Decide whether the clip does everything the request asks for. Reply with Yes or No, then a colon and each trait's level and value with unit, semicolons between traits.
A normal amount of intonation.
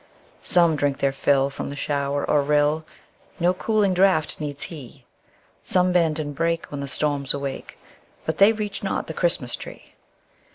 Yes: average, 3.9 semitones